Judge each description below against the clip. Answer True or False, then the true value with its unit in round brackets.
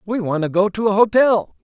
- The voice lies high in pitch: True (200 Hz)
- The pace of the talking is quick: True (245 wpm)